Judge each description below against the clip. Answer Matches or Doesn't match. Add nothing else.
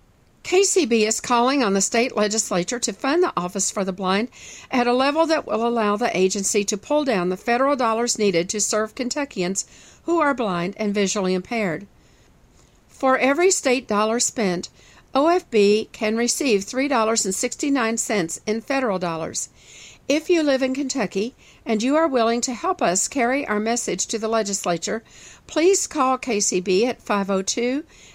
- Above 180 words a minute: Doesn't match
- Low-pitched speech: Doesn't match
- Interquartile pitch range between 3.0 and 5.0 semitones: Matches